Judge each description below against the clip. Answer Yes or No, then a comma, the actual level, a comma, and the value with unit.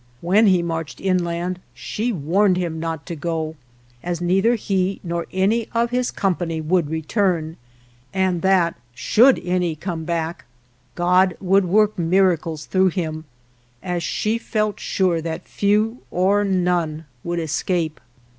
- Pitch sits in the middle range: Yes, medium, 180 Hz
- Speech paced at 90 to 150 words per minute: Yes, average, 140 wpm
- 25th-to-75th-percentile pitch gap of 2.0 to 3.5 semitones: Yes, average, 2.9 semitones